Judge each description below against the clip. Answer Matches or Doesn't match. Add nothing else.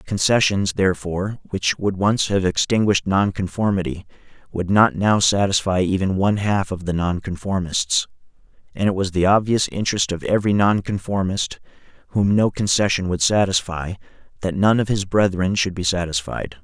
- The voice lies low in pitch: Matches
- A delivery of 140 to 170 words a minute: Matches